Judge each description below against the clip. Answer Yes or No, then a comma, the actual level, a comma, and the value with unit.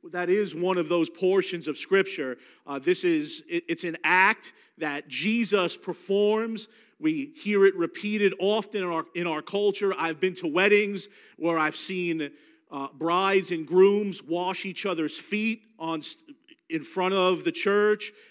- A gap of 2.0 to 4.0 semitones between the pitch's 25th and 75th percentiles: Yes, average, 3.5 semitones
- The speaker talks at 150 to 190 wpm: Yes, average, 160 wpm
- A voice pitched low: No, high, 190 Hz